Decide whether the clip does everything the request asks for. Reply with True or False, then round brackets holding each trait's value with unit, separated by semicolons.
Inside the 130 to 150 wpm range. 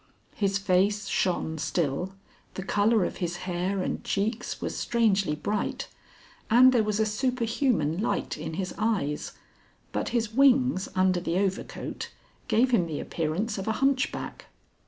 True (145 wpm)